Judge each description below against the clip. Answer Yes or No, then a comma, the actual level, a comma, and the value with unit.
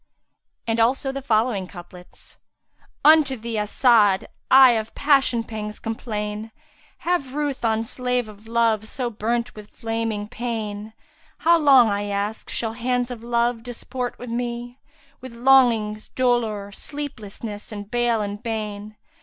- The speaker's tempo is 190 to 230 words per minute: No, average, 140 wpm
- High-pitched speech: Yes, high, 230 Hz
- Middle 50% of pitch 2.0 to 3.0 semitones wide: Yes, average, 2.7 semitones